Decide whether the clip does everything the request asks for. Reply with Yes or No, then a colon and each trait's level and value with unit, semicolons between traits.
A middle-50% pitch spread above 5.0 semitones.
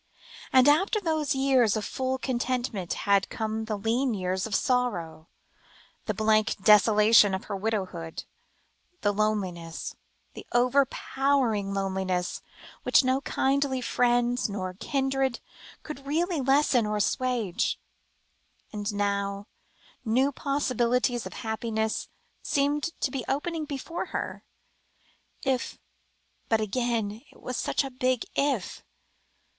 No: average, 4.6 semitones